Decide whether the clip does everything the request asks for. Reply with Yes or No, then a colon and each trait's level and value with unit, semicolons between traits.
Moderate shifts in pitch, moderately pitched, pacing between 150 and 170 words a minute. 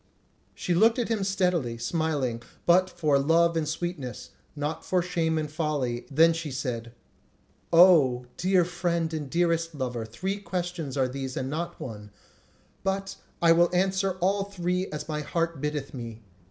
Yes: average, 4.6 semitones; medium, 165 Hz; average, 155 wpm